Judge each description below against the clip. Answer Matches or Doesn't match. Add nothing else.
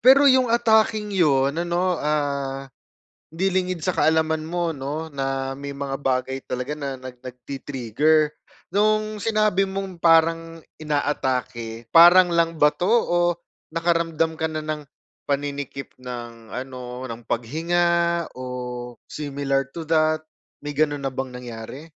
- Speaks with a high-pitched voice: Doesn't match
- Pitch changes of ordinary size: Matches